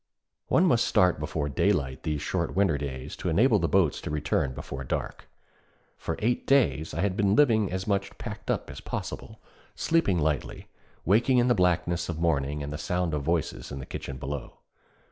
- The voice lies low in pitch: Yes, very low, 85 Hz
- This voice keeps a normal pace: Yes, average, 185 wpm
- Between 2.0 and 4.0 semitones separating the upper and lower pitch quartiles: No, average, 5.2 semitones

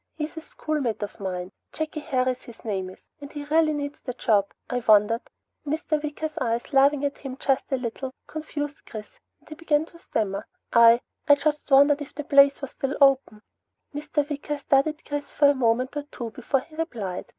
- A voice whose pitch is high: Yes, very high, 280 Hz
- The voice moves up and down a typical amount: Yes, average, 4.2 semitones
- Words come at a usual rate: Yes, average, 195 wpm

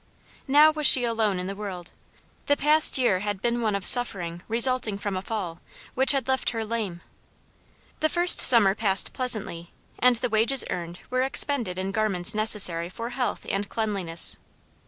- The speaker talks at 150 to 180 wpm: Yes, average, 170 wpm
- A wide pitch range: No, average, 4.8 semitones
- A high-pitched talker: Yes, high, 215 Hz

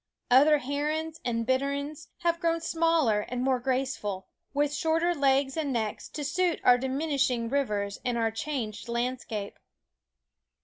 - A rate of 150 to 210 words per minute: No, slow, 135 wpm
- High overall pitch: Yes, very high, 270 Hz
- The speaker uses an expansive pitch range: No, average, 4.2 semitones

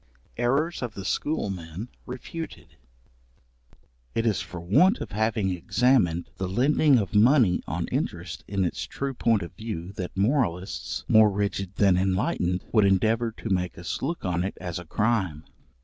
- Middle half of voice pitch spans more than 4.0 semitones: Yes, average, 4.8 semitones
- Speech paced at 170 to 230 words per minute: No, average, 155 wpm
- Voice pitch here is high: No, low, 100 Hz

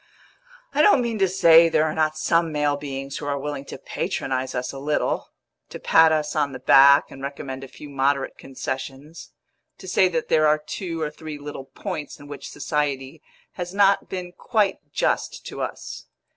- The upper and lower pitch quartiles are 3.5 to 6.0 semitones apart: No, average, 3.1 semitones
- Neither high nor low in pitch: Yes, medium, 150 Hz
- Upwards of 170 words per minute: Yes, average, 185 wpm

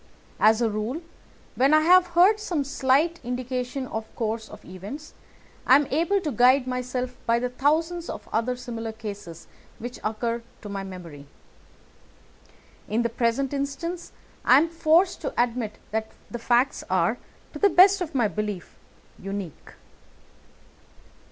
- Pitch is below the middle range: No, very high, 250 Hz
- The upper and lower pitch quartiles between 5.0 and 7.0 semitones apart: Yes, wide, 5.6 semitones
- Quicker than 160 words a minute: No, average, 150 wpm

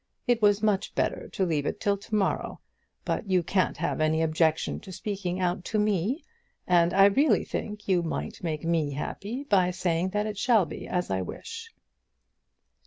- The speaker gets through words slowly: No, average, 180 wpm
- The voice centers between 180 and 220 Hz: Yes, high, 190 Hz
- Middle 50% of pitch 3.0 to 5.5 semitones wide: Yes, average, 3.7 semitones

